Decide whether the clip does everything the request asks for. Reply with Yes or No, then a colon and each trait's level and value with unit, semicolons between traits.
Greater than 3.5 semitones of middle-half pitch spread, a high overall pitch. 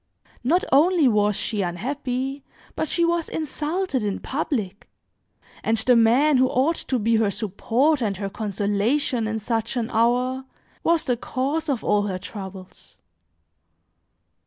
Yes: average, 5.3 semitones; high, 245 Hz